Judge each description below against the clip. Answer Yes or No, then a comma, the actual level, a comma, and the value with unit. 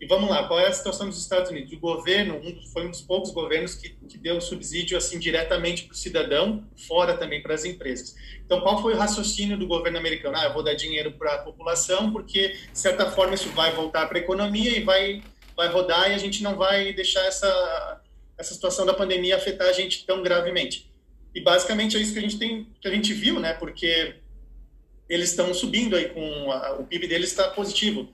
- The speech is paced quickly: Yes, fast, 220 wpm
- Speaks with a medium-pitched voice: Yes, medium, 180 Hz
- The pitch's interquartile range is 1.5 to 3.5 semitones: Yes, average, 3.0 semitones